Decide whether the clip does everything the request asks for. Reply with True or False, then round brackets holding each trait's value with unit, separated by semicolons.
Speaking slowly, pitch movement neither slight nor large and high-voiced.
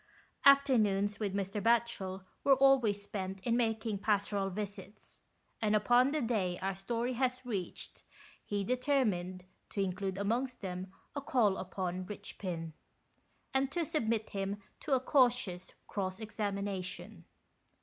True (130 wpm; 4.1 semitones; 205 Hz)